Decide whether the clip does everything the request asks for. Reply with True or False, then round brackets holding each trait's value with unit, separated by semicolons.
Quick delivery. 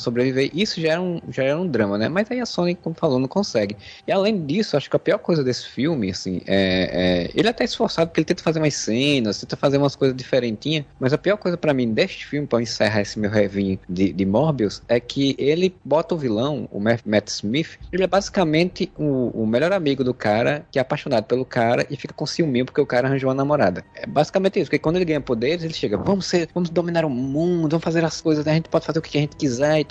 True (255 wpm)